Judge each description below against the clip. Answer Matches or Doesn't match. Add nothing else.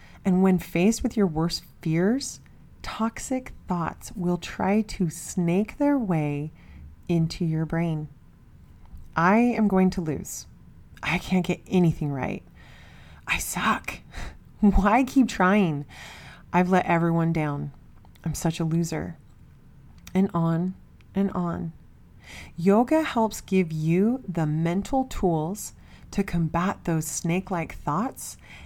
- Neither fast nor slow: Doesn't match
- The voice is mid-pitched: Matches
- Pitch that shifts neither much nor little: Matches